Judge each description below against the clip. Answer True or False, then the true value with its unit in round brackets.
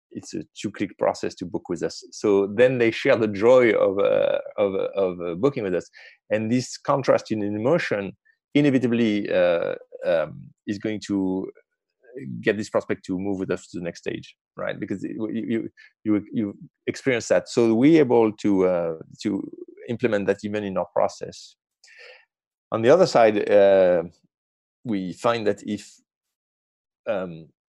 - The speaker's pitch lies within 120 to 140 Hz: False (105 Hz)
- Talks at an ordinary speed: True (160 wpm)